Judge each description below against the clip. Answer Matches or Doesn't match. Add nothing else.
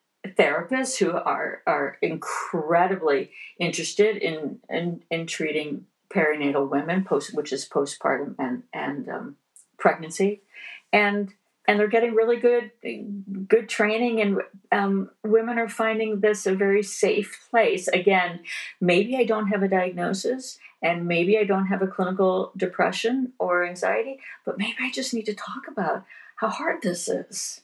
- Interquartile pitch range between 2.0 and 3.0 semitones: Doesn't match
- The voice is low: Doesn't match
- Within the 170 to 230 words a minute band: Doesn't match